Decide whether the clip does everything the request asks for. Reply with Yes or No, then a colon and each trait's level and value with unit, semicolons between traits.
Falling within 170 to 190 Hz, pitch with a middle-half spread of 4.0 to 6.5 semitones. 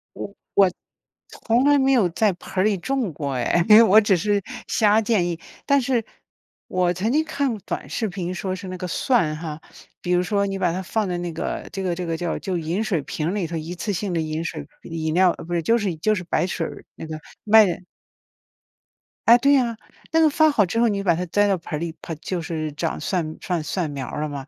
Yes: medium, 185 Hz; average, 4.5 semitones